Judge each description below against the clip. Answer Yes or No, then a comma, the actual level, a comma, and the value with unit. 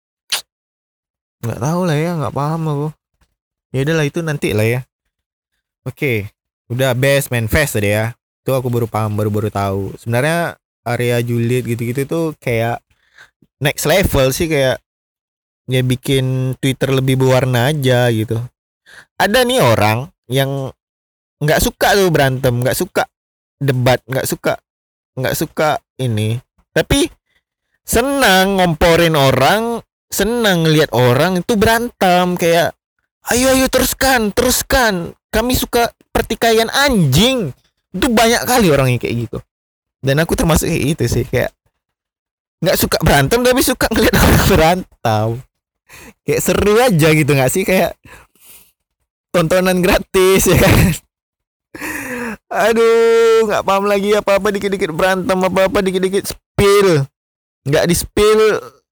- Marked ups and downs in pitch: Yes, wide, 8.7 semitones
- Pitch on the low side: No, medium, 155 Hz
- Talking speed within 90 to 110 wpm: No, average, 130 wpm